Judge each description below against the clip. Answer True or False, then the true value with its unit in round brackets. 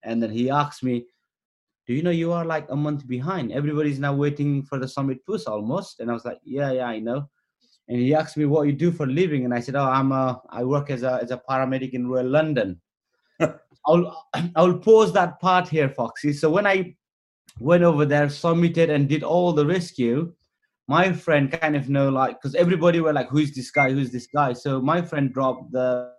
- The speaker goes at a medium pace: False (225 wpm)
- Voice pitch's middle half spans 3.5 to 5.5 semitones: True (4.2 semitones)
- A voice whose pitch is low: False (145 Hz)